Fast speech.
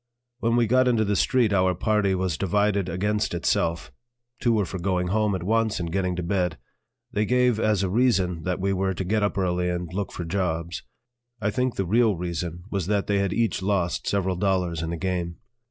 Yes: fast, 210 wpm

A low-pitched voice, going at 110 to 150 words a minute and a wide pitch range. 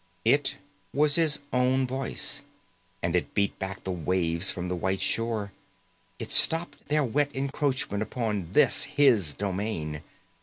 Yes: low, 110 Hz; average, 140 wpm; wide, 7.0 semitones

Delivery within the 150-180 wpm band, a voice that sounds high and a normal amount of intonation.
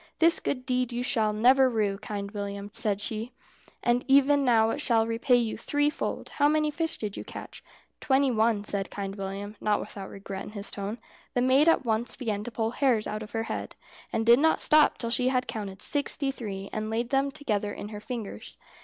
No: fast, 205 wpm; high, 230 Hz; average, 4.0 semitones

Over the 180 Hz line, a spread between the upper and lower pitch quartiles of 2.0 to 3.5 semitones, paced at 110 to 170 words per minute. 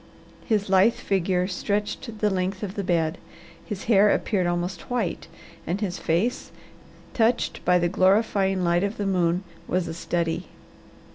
Yes: high, 190 Hz; average, 2.8 semitones; average, 150 wpm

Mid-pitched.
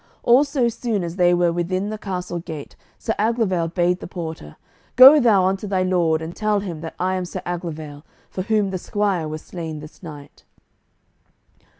Yes: medium, 180 Hz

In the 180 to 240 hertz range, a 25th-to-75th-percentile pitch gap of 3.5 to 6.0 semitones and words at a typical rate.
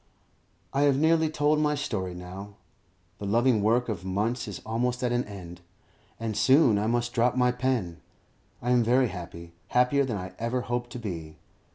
No: low, 120 Hz; average, 4.1 semitones; average, 180 wpm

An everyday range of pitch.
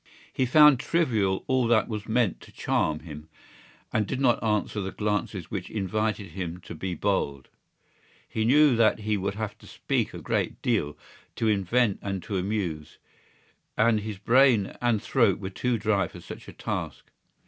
Yes: average, 3.5 semitones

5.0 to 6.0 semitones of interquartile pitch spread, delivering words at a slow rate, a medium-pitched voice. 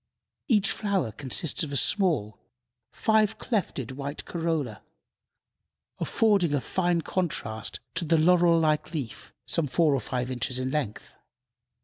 Yes: wide, 5.4 semitones; slow, 130 wpm; medium, 155 Hz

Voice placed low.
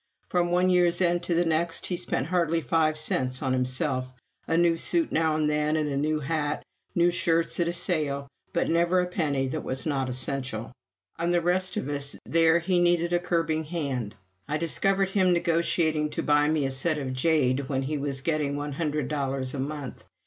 No: medium, 155 Hz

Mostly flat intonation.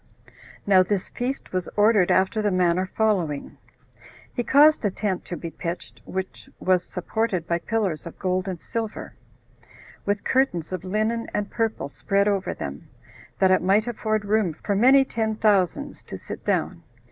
No: average, 3.1 semitones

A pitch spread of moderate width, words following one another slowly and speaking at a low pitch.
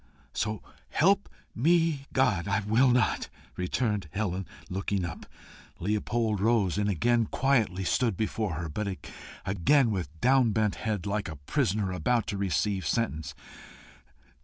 Yes: average, 4.0 semitones; slow, 130 wpm; low, 105 Hz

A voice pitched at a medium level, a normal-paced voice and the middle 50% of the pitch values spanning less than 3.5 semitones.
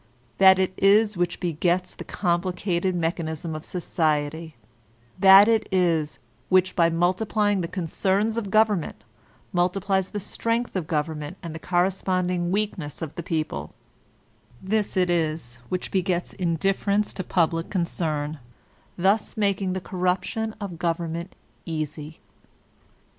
No: medium, 180 Hz; slow, 125 wpm; average, 2.9 semitones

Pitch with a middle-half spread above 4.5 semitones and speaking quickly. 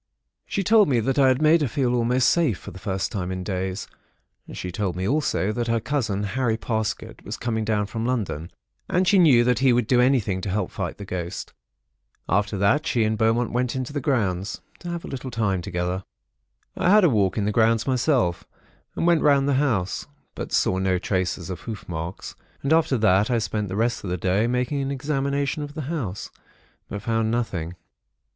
Yes: wide, 5.6 semitones; fast, 210 wpm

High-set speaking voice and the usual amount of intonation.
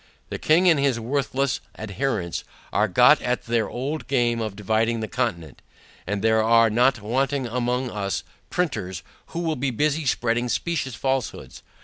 No: low, 120 Hz; average, 3.8 semitones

